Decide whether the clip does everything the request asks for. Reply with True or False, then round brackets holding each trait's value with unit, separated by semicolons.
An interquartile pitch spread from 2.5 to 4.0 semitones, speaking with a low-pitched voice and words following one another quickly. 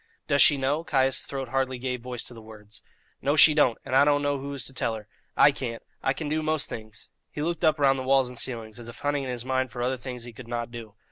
True (3.0 semitones; 130 Hz; 275 wpm)